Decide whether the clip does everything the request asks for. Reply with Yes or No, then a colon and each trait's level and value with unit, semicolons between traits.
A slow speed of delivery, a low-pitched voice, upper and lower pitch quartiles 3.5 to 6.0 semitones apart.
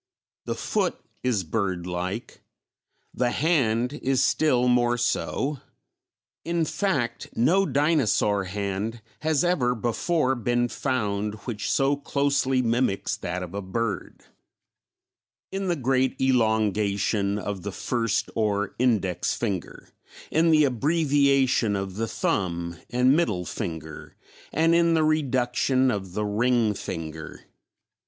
Yes: slow, 120 wpm; low, 120 Hz; average, 5.2 semitones